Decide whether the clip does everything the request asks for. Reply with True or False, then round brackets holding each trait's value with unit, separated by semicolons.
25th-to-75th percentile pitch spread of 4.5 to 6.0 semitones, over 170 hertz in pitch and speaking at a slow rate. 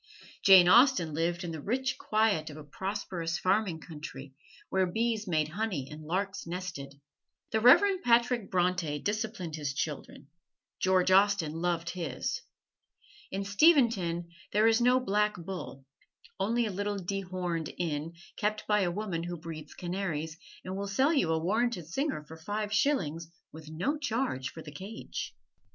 False (4.8 semitones; 185 Hz; 150 wpm)